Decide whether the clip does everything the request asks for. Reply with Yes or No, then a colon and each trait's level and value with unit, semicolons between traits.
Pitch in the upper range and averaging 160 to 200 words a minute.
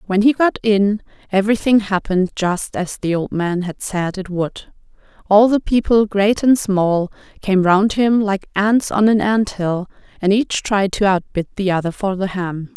Yes: high, 200 Hz; average, 190 wpm